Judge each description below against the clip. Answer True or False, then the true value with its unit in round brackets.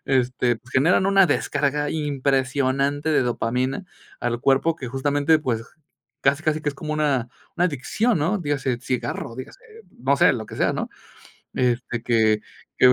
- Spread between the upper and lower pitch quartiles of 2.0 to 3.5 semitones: True (3.2 semitones)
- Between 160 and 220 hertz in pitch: False (135 Hz)